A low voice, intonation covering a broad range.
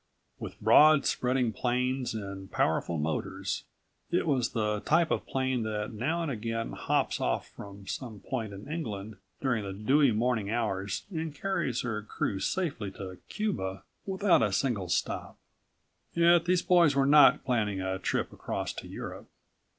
Yes: low, 120 Hz; wide, 6.2 semitones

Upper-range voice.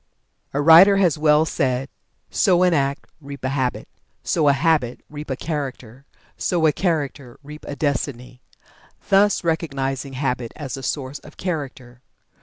No: medium, 140 Hz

